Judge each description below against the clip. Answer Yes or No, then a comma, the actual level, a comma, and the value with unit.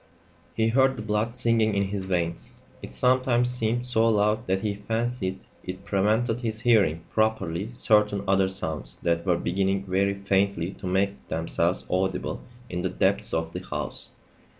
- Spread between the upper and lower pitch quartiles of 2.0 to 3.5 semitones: Yes, average, 3.2 semitones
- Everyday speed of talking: Yes, average, 160 wpm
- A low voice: Yes, low, 100 Hz